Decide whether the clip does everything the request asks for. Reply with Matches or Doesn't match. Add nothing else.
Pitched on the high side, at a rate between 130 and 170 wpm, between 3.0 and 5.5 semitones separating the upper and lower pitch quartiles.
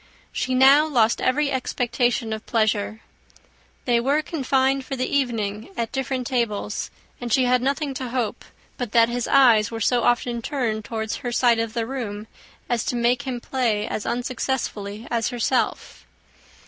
Doesn't match